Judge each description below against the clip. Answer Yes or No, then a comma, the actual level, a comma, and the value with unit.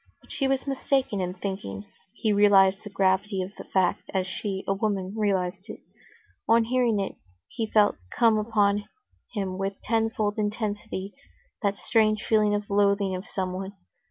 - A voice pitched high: Yes, high, 205 Hz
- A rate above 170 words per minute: No, average, 155 wpm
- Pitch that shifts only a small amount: Yes, narrow, 2.1 semitones